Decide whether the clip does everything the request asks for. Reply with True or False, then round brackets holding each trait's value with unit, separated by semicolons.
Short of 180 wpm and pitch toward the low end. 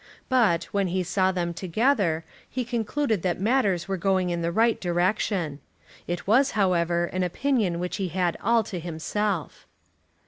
False (160 wpm; 185 Hz)